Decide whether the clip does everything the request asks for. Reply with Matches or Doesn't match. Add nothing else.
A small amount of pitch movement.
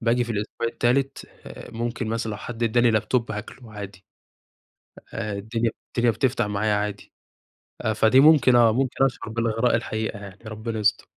Matches